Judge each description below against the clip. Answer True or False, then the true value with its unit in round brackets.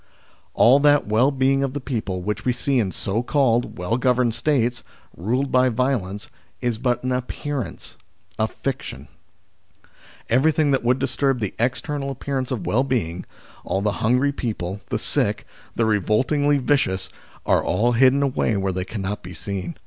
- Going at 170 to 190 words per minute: False (160 wpm)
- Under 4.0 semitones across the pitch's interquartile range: False (4.3 semitones)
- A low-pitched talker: True (125 Hz)